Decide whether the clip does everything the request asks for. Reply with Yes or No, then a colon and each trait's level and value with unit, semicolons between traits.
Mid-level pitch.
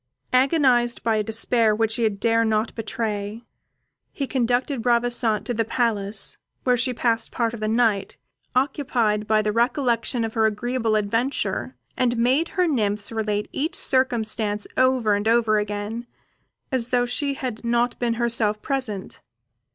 No: high, 230 Hz